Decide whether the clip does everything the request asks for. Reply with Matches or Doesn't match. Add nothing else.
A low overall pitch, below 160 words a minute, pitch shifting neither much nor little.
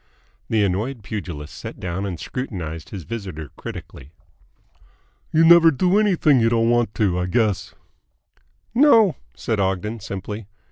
Doesn't match